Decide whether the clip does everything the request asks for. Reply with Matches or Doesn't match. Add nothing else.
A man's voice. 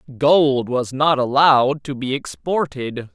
Matches